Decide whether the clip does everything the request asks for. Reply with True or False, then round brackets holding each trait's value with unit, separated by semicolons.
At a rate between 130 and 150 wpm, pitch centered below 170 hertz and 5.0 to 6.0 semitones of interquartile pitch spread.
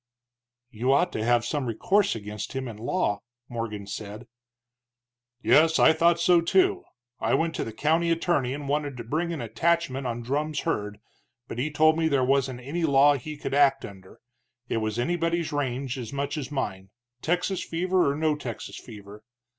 False (180 wpm; 140 Hz; 5.5 semitones)